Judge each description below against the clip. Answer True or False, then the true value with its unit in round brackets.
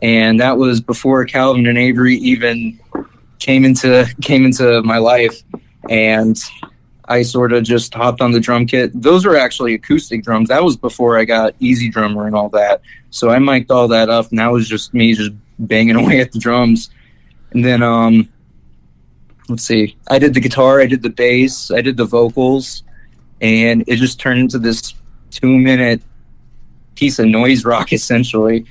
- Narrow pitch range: True (2.2 semitones)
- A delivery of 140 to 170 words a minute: False (180 wpm)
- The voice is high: False (120 Hz)